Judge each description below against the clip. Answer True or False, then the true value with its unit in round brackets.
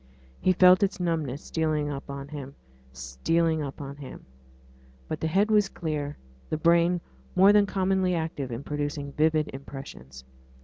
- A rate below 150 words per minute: True (140 wpm)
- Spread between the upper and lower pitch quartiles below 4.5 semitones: True (4.1 semitones)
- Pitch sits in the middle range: True (155 Hz)